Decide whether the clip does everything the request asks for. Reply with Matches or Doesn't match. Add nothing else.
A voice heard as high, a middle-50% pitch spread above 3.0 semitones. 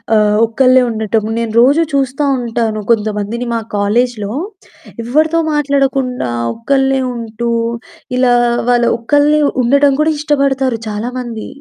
Matches